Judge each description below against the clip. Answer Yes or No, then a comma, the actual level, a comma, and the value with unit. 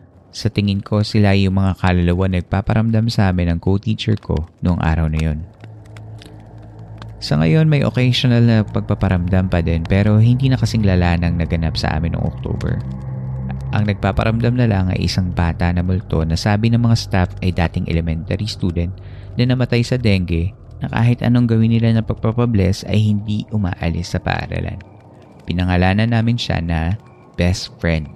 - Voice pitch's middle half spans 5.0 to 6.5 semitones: No, average, 4.2 semitones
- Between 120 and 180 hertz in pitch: No, low, 100 Hz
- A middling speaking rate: No, fast, 160 wpm